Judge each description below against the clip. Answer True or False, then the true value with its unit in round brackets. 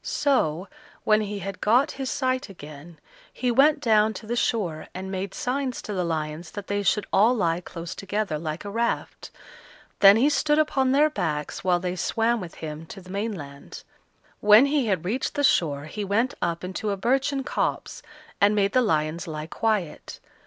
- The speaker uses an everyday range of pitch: False (5.9 semitones)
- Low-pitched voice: False (205 Hz)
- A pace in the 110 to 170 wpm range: False (185 wpm)